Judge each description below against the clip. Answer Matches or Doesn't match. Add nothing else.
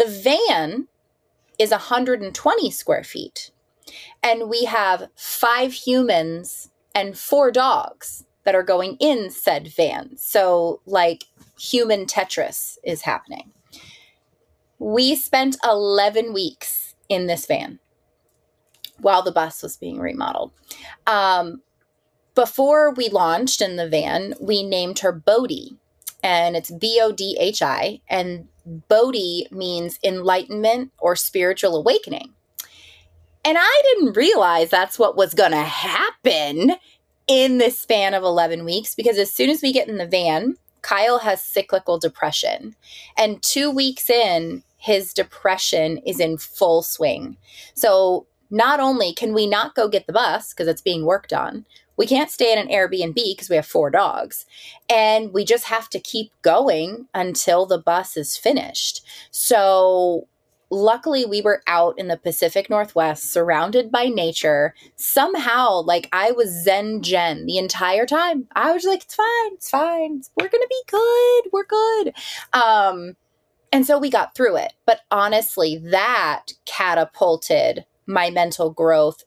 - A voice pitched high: Matches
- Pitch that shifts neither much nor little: Doesn't match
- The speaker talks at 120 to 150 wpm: Matches